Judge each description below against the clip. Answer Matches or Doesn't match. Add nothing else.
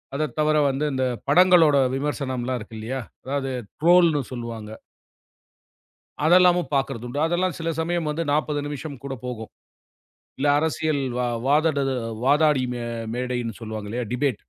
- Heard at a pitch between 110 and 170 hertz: Matches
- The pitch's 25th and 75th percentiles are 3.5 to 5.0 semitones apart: Matches